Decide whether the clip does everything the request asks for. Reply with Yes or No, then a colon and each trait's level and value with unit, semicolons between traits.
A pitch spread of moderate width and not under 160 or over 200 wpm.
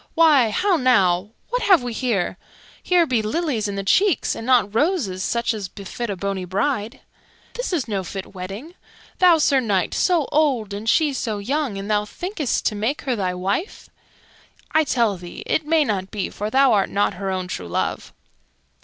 No: wide, 7.0 semitones; average, 190 wpm